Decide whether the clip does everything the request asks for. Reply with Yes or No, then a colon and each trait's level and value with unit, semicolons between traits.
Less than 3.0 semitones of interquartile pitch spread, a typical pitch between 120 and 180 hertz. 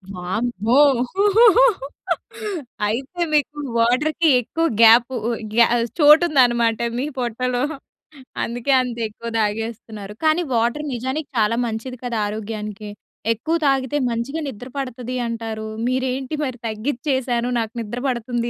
No: narrow, 2.6 semitones; high, 240 Hz